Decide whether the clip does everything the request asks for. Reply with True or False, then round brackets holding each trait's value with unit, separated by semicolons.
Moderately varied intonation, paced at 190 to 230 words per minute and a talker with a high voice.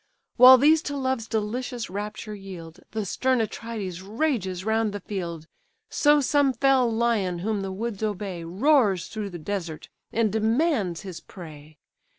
False (4.7 semitones; 150 wpm; 215 Hz)